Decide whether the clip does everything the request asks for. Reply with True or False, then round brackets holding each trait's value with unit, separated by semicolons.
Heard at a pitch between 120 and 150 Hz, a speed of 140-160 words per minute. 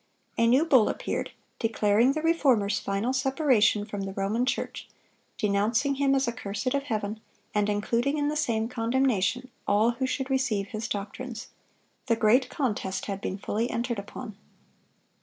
False (230 Hz; 155 wpm)